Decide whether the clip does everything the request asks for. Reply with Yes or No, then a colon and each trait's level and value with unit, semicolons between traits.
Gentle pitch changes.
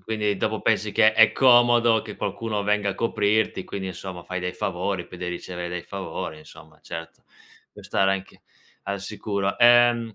No: average, 3.2 semitones